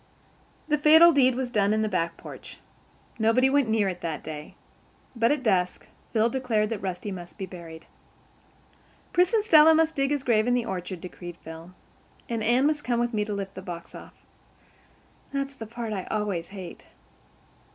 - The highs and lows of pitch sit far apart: Yes, wide, 6.1 semitones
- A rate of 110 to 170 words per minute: No, average, 185 wpm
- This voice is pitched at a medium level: No, high, 220 Hz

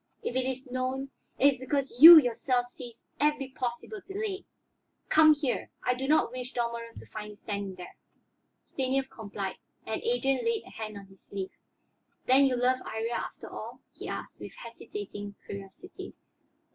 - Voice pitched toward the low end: No, very high, 255 Hz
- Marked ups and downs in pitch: No, average, 3.8 semitones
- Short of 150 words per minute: No, average, 165 wpm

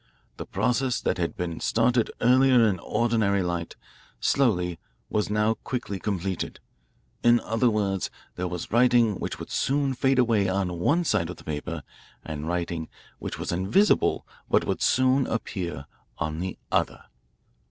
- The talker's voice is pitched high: No, low, 105 Hz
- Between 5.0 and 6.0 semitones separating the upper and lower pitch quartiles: Yes, wide, 5.6 semitones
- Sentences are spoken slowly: No, average, 150 wpm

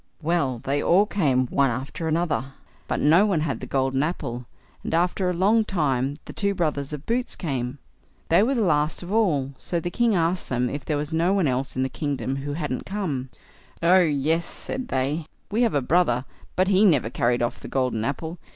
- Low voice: No, medium, 150 Hz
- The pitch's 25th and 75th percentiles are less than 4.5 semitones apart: No, average, 5.1 semitones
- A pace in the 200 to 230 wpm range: Yes, fast, 205 wpm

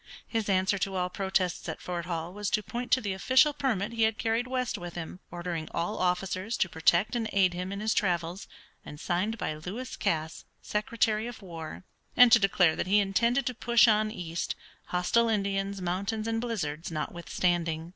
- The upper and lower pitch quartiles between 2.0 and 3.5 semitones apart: No, average, 4.2 semitones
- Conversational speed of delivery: Yes, average, 185 wpm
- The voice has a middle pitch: No, high, 195 Hz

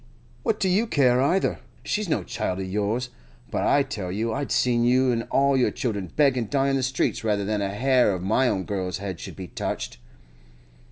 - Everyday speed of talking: No, fast, 215 wpm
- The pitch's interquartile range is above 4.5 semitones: Yes, average, 5.1 semitones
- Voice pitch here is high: No, low, 120 Hz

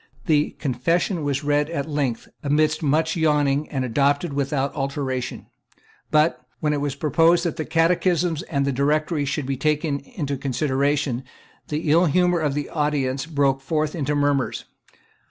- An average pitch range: No, narrow, 2.3 semitones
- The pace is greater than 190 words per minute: No, average, 155 wpm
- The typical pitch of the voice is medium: Yes, medium, 145 Hz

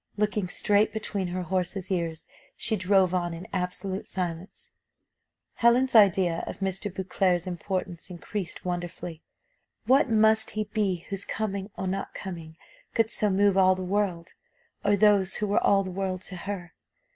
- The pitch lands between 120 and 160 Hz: No, high, 190 Hz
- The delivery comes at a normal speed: Yes, average, 155 wpm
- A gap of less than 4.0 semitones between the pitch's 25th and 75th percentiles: Yes, narrow, 2.4 semitones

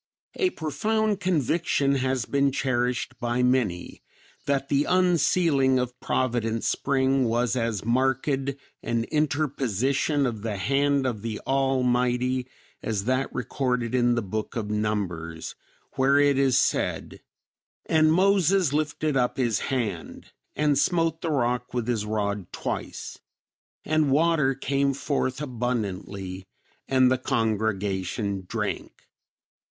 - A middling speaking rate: No, slow, 120 wpm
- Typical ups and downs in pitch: Yes, average, 3.7 semitones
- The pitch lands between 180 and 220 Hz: No, low, 130 Hz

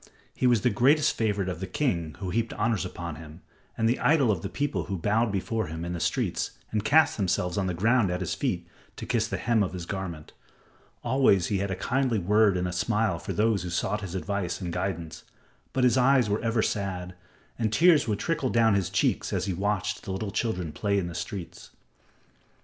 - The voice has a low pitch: Yes, low, 100 Hz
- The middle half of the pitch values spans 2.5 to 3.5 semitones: No, average, 4.2 semitones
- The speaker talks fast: Yes, fast, 220 wpm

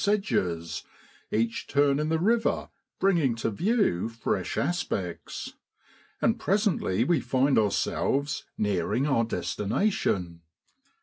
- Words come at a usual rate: No, slow, 105 wpm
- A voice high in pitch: No, low, 135 Hz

